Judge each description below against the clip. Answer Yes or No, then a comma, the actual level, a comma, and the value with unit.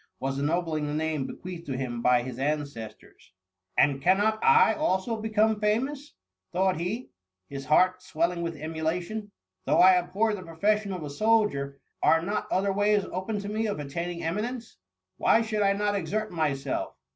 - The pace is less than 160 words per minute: No, average, 175 wpm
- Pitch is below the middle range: No, medium, 180 Hz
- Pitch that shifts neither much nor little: No, wide, 5.7 semitones